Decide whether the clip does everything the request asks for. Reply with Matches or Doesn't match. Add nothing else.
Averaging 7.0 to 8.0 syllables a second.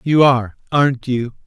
Doesn't match